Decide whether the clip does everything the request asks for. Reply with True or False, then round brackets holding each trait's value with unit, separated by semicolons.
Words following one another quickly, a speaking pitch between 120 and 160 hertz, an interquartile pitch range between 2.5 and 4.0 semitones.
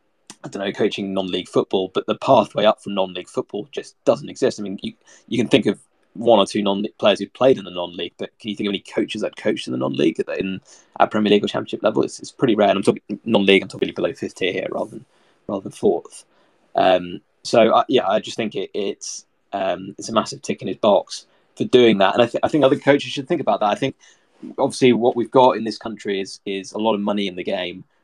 False (260 wpm; 105 Hz; 3.6 semitones)